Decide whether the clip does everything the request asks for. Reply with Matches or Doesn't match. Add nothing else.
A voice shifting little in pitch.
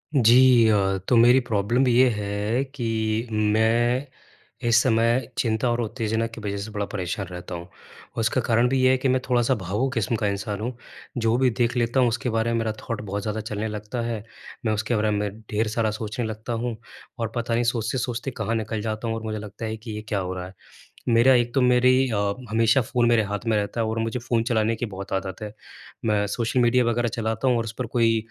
Matches